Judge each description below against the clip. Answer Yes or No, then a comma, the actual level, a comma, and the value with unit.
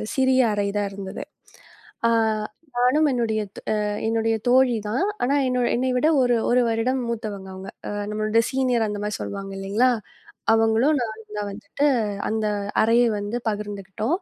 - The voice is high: Yes, high, 225 Hz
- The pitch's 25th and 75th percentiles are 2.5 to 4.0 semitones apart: Yes, average, 3.2 semitones